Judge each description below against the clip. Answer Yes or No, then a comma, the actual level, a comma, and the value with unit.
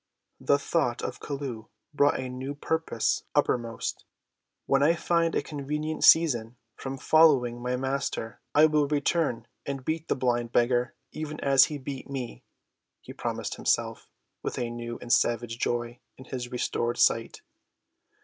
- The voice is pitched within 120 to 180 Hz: Yes, low, 135 Hz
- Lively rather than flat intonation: No, average, 3.6 semitones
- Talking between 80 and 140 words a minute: No, average, 150 wpm